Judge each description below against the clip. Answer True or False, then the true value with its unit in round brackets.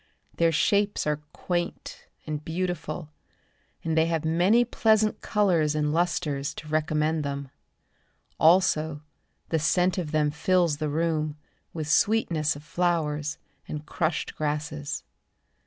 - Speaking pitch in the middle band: True (160 Hz)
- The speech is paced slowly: True (125 wpm)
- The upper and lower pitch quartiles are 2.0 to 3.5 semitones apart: True (2.7 semitones)